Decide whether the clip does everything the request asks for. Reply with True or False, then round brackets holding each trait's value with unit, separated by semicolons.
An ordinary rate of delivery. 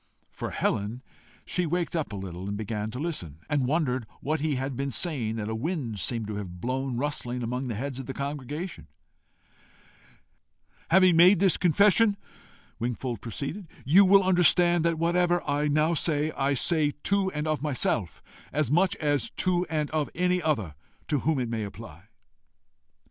True (165 wpm)